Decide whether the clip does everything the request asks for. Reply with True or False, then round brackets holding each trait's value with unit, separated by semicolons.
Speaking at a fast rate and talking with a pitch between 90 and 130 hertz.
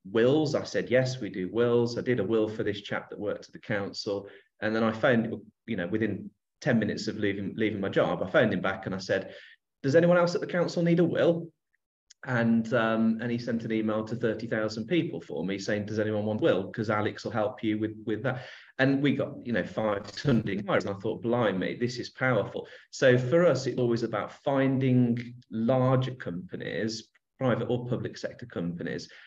True (210 wpm; 115 Hz)